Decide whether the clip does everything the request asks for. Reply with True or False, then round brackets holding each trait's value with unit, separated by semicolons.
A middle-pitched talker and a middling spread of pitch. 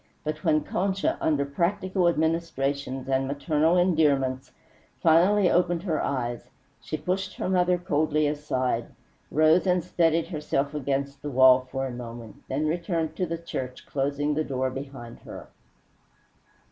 True (150 Hz; 4.0 semitones)